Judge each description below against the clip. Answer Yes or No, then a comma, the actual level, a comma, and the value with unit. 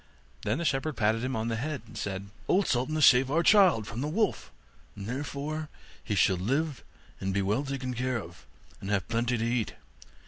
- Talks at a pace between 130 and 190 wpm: No, fast, 205 wpm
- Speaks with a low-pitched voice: Yes, low, 125 Hz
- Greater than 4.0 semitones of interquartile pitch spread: Yes, wide, 5.4 semitones